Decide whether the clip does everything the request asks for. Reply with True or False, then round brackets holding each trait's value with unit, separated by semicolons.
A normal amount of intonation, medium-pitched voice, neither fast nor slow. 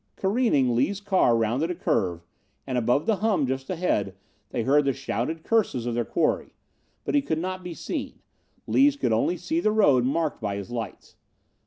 False (7.7 semitones; 145 Hz; 185 wpm)